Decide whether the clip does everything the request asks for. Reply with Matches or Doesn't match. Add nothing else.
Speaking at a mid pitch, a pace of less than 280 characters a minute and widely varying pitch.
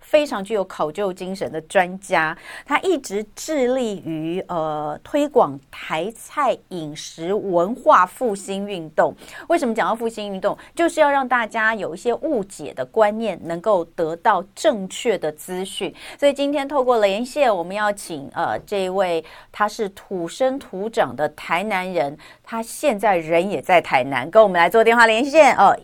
Doesn't match